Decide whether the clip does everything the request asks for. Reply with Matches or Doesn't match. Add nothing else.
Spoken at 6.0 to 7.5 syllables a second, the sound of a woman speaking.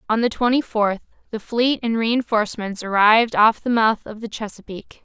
Doesn't match